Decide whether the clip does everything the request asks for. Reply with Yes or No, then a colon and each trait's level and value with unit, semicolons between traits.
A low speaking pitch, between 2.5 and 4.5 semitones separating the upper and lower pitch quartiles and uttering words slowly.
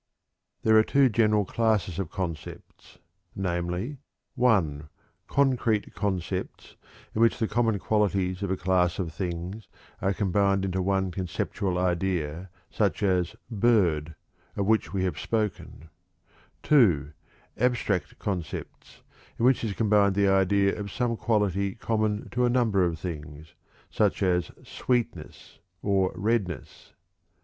Yes: low, 100 Hz; average, 3.5 semitones; slow, 125 wpm